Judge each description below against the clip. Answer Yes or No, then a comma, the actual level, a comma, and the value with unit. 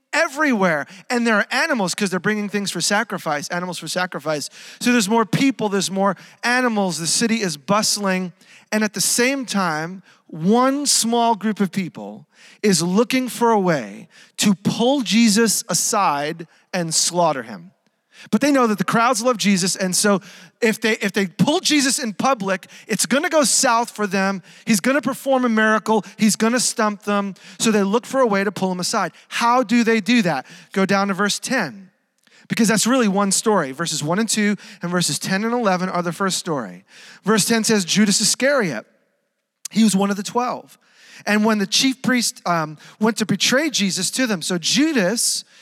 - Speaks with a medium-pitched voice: No, high, 210 Hz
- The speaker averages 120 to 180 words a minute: No, average, 190 wpm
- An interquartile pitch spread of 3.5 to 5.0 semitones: Yes, average, 3.9 semitones